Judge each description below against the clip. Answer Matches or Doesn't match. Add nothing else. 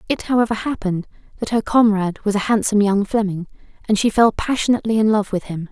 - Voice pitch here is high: Matches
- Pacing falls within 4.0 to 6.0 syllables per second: Doesn't match